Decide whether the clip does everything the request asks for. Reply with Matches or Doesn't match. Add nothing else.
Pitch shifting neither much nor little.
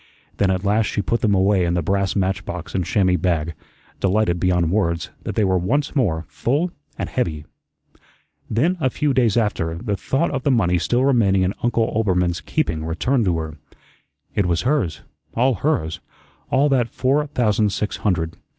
Doesn't match